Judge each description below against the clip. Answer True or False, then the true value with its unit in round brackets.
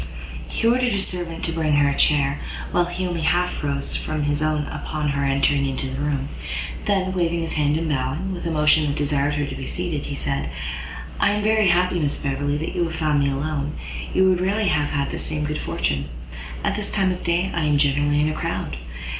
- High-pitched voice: False (150 Hz)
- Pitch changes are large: False (3.5 semitones)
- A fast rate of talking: True (225 wpm)